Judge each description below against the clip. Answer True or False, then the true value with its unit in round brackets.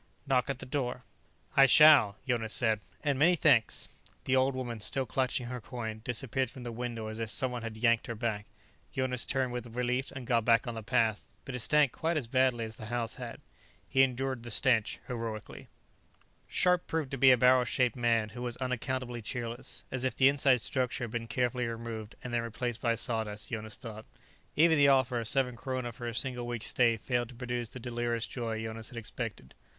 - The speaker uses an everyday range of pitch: False (2.2 semitones)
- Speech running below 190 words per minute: False (205 wpm)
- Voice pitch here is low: True (120 Hz)